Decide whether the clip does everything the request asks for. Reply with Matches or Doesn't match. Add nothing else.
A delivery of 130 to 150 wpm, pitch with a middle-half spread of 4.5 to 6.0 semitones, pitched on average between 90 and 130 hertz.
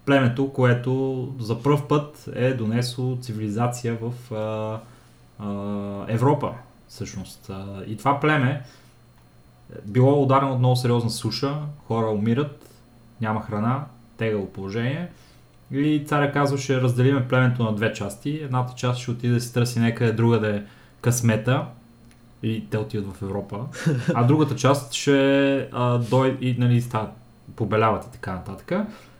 Doesn't match